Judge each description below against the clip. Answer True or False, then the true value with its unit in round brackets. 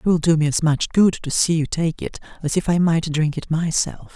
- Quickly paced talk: True (275 wpm)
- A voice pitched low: False (160 Hz)